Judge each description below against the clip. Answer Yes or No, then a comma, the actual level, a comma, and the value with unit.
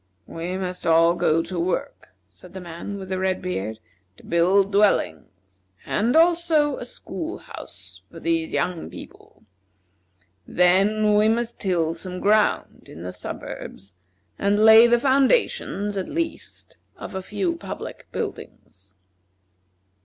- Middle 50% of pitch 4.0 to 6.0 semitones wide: Yes, average, 4.8 semitones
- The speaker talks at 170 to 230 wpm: No, slow, 135 wpm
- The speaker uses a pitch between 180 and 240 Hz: Yes, high, 190 Hz